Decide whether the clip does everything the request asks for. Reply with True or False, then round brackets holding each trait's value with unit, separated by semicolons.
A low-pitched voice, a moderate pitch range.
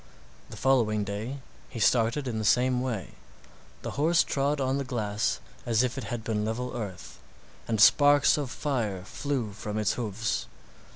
True (120 Hz; 3.9 semitones)